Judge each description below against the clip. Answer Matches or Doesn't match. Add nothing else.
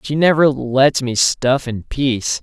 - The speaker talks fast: Doesn't match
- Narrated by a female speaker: Doesn't match